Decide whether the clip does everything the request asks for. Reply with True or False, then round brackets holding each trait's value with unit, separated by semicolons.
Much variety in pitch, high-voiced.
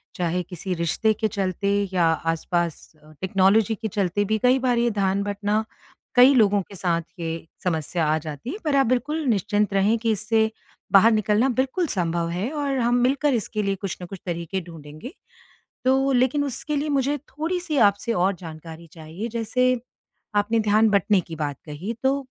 True (5.9 semitones; 205 Hz)